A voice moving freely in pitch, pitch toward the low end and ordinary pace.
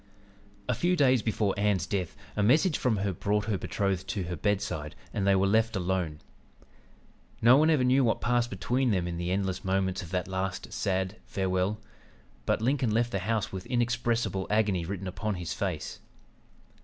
No: average, 3.8 semitones; low, 100 Hz; average, 180 wpm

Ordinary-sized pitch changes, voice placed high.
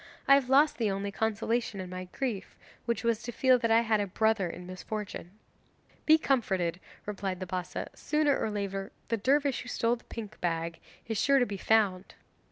Yes: average, 4.1 semitones; high, 215 Hz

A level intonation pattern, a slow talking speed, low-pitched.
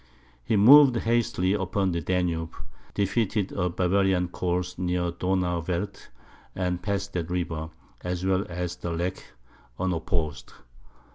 Yes: narrow, 1.8 semitones; slow, 120 wpm; very low, 90 Hz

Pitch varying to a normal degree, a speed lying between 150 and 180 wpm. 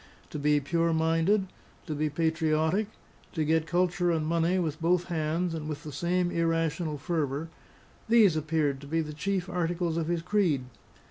No: narrow, 2.2 semitones; average, 165 wpm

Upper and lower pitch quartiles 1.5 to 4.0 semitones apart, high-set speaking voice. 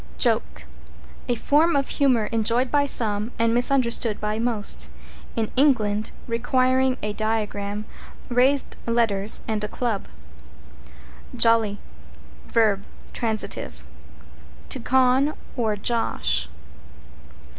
Yes: average, 3.2 semitones; high, 230 Hz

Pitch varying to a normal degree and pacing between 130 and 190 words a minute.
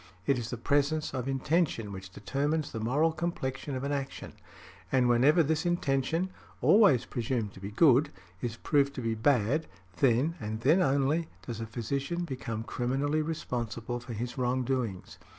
Yes: average, 4.2 semitones; average, 160 wpm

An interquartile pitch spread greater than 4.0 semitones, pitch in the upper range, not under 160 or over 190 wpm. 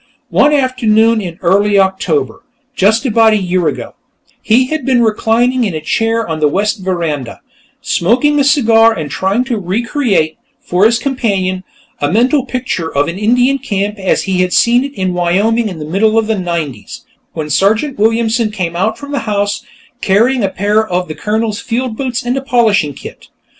Yes: average, 4.4 semitones; high, 215 Hz; average, 180 wpm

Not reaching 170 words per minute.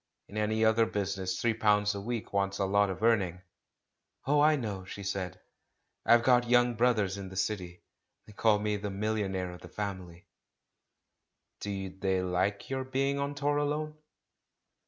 No: average, 175 wpm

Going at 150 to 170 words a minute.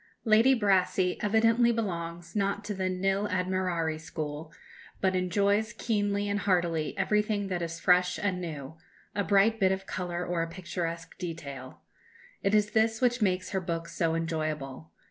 Yes: average, 155 wpm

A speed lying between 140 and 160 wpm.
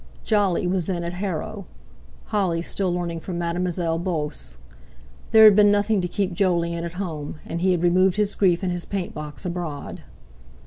No: average, 175 wpm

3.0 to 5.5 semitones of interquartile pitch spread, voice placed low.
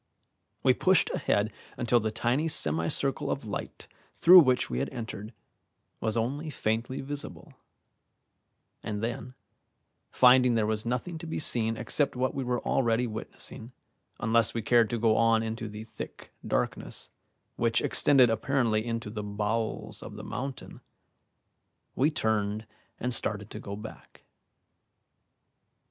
No: narrow, 2.6 semitones; low, 115 Hz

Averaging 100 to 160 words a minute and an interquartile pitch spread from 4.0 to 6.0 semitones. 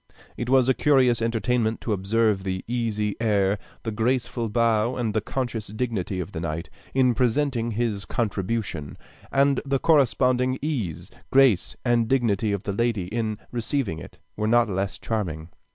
No: average, 155 wpm; average, 3.4 semitones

